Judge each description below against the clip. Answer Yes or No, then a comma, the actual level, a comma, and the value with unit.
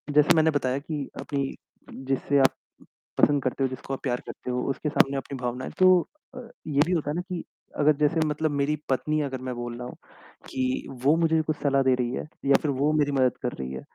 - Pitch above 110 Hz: Yes, medium, 140 Hz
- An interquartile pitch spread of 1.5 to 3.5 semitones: Yes, average, 2.8 semitones